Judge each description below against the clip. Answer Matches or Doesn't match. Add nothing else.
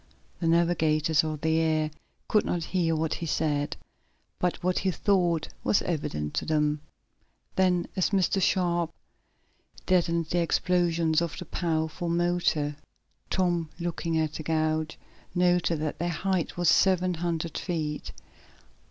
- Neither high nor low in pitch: Matches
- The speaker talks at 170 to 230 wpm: Doesn't match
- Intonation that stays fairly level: Matches